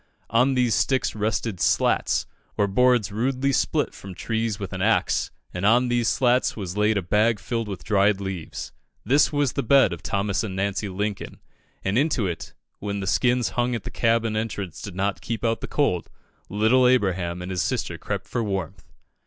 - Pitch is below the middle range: Yes, low, 105 Hz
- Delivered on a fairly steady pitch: No, average, 3.8 semitones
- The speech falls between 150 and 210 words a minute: Yes, average, 185 wpm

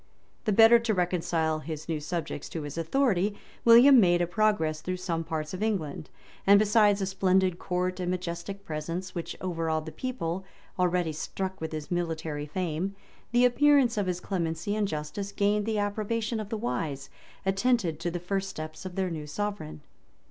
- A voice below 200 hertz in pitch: Yes, medium, 185 Hz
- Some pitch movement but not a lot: Yes, average, 4.2 semitones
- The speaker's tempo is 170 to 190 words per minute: Yes, average, 175 wpm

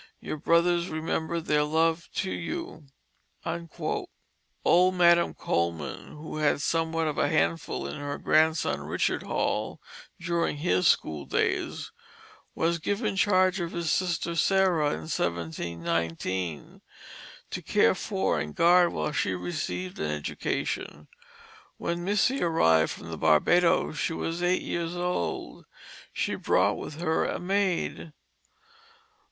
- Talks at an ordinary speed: No, slow, 125 wpm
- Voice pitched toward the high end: No, medium, 160 Hz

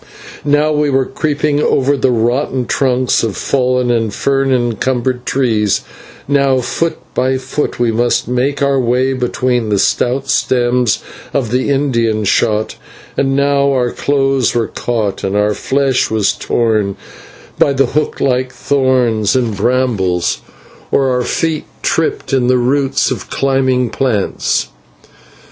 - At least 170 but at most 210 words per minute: No, average, 140 wpm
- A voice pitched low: Yes, low, 130 Hz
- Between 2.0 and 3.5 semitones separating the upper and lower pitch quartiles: Yes, narrow, 2.5 semitones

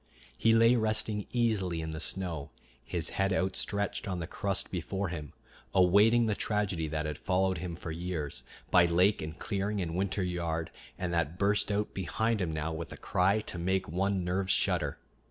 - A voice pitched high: No, very low, 95 Hz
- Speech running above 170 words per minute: Yes, average, 180 wpm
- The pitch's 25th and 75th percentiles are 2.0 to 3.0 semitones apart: No, average, 3.4 semitones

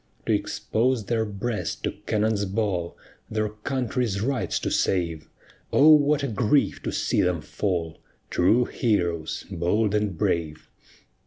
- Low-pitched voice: Yes, low, 105 Hz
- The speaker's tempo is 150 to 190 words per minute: No, slow, 135 wpm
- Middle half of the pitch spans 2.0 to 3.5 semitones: No, average, 5.2 semitones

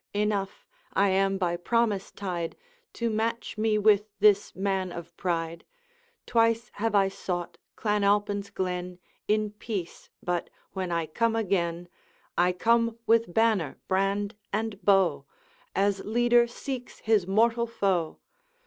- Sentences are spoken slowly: Yes, slow, 130 wpm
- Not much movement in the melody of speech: No, average, 3.5 semitones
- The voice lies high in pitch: Yes, high, 200 Hz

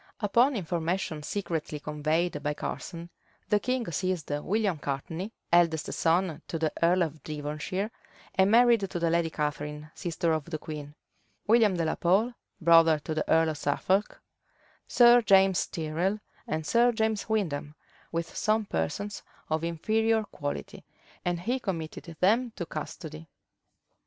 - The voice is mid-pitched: Yes, medium, 170 Hz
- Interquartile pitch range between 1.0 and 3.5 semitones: No, average, 4.7 semitones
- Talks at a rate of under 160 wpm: Yes, average, 140 wpm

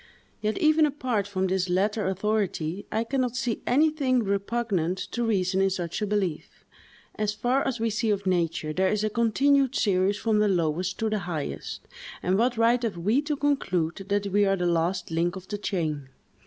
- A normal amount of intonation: Yes, average, 4.1 semitones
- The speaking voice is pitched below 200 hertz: No, high, 205 Hz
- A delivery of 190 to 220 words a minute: Yes, average, 195 wpm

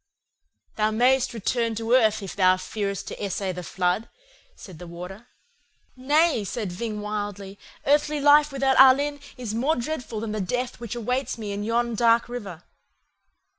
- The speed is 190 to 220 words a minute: No, average, 160 wpm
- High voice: Yes, high, 225 Hz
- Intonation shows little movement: No, average, 4.0 semitones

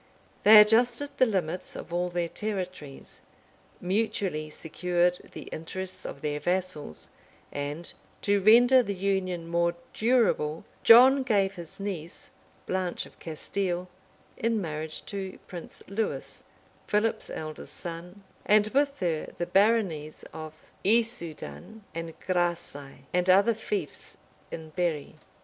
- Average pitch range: Yes, average, 4.1 semitones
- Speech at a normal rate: No, slow, 120 wpm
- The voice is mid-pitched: Yes, medium, 180 Hz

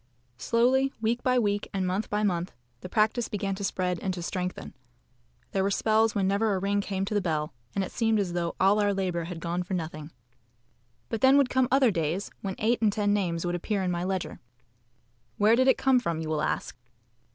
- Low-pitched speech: No, high, 195 Hz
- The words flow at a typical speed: No, fast, 220 wpm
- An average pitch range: Yes, average, 3.6 semitones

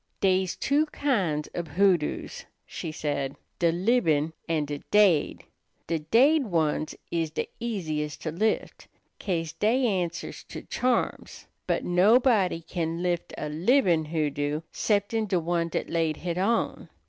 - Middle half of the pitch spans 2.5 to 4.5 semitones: No, average, 5.0 semitones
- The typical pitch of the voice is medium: Yes, medium, 175 Hz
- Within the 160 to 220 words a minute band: No, slow, 135 wpm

